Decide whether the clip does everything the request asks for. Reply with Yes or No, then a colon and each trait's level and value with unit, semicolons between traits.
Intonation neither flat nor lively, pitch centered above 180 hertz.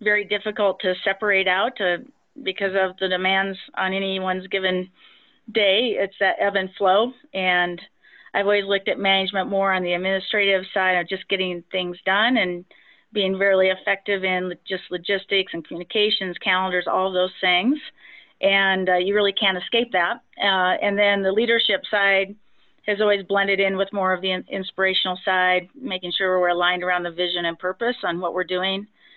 No: narrow, 1.5 semitones; high, 190 Hz